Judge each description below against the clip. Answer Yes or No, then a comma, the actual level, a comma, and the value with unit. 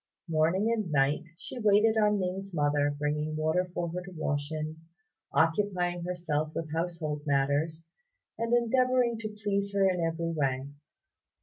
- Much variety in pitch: No, average, 4.6 semitones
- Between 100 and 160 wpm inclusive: Yes, average, 145 wpm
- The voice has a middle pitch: Yes, medium, 170 Hz